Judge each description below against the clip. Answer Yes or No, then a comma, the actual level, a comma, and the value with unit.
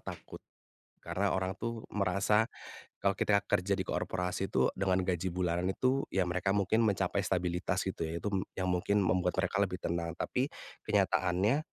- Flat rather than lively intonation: Yes, narrow, 1.9 semitones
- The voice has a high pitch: No, very low, 95 Hz